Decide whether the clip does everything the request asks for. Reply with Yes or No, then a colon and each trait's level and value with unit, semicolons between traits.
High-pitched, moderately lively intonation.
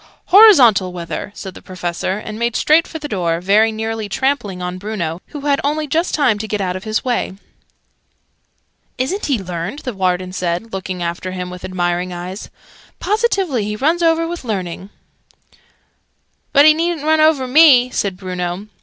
No: high, 215 Hz; wide, 7.9 semitones